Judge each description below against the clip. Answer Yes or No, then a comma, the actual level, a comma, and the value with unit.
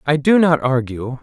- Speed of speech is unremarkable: Yes, average, 195 wpm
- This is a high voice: No, medium, 140 Hz